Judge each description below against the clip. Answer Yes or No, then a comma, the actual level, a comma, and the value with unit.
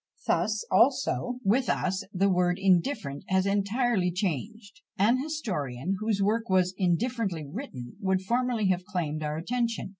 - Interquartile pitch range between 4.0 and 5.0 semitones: Yes, average, 4.4 semitones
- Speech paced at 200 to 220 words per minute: No, average, 140 wpm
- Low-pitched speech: No, high, 195 Hz